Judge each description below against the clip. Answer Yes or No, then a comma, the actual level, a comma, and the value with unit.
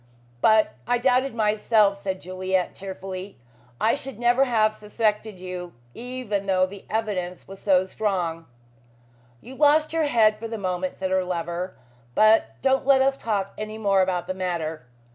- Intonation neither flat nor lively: Yes, average, 3.7 semitones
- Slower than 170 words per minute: Yes, average, 160 wpm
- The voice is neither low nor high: No, high, 205 Hz